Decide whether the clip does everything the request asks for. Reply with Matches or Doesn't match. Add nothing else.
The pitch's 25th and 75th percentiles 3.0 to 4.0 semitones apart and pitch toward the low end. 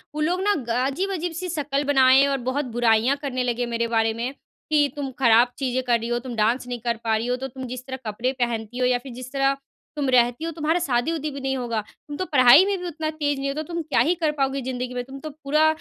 Doesn't match